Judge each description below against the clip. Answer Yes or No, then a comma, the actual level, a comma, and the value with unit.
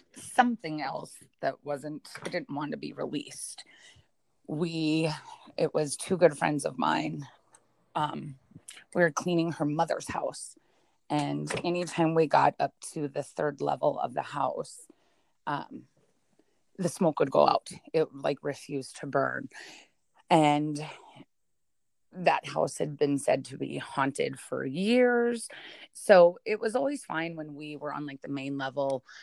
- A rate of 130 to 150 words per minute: Yes, average, 145 wpm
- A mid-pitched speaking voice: Yes, medium, 160 Hz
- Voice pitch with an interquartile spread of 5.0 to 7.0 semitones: No, average, 3.5 semitones